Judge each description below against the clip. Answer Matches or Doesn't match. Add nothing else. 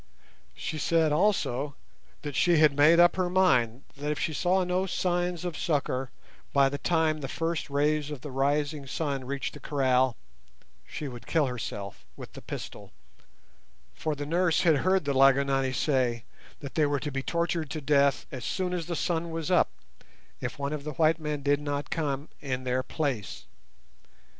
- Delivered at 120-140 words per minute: Doesn't match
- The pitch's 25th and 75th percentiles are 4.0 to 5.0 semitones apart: Doesn't match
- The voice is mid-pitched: Matches